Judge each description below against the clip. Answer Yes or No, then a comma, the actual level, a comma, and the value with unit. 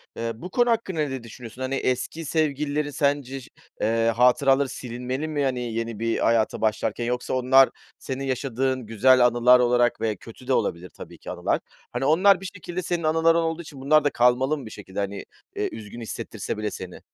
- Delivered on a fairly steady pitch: No, average, 4.0 semitones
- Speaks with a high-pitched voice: No, low, 130 Hz